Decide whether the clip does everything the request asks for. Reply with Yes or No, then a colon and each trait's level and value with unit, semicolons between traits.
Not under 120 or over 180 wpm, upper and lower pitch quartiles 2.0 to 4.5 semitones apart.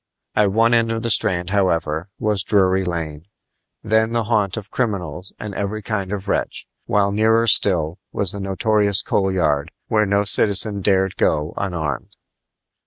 Yes: average, 160 wpm; average, 2.9 semitones